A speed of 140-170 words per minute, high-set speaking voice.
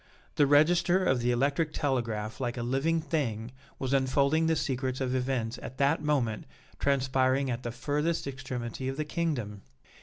No: average, 160 wpm; low, 135 Hz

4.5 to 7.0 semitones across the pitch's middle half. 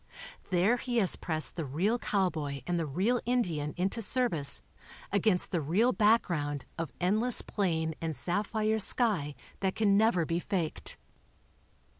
Yes: average, 5.3 semitones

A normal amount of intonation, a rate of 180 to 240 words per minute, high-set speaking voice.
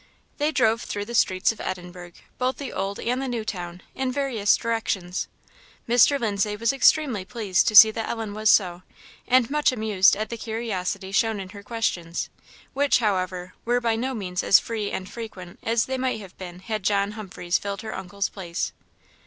Yes: average, 3.8 semitones; average, 185 wpm; high, 215 Hz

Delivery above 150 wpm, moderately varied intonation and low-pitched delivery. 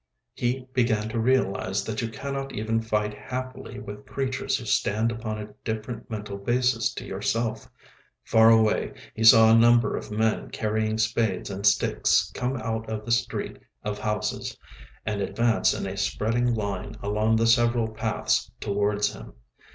No: average, 160 wpm; narrow, 1.9 semitones; low, 110 Hz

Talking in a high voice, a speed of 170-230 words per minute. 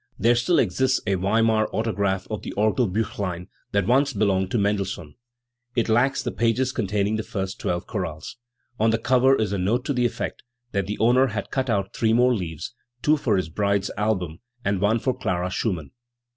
No: low, 105 Hz; average, 185 wpm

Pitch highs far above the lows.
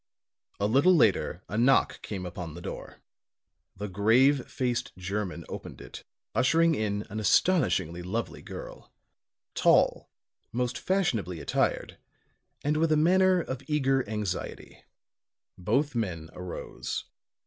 Yes: wide, 7.6 semitones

